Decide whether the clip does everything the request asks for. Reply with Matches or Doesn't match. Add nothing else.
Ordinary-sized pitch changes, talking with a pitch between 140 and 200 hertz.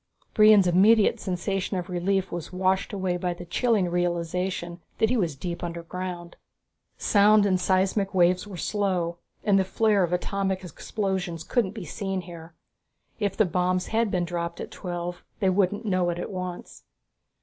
Doesn't match